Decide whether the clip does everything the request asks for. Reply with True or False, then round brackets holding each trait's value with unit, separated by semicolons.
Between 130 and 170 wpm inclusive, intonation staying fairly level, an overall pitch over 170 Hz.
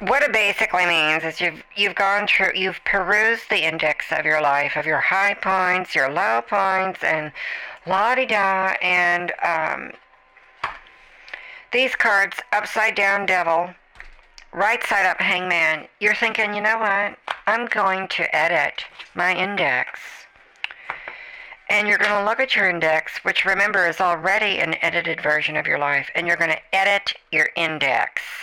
False (150 wpm; 3.7 semitones; 190 Hz)